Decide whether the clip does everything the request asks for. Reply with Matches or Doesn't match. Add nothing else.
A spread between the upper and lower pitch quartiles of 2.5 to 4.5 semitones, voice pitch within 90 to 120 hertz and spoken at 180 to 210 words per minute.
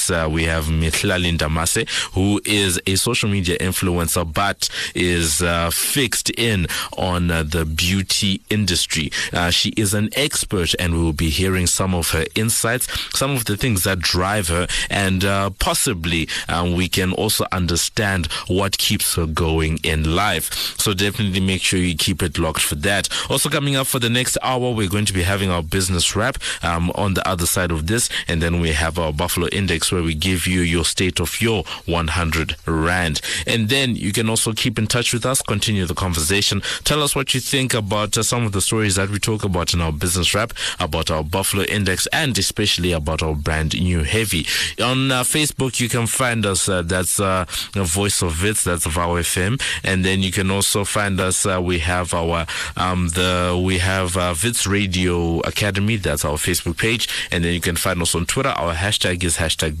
Matches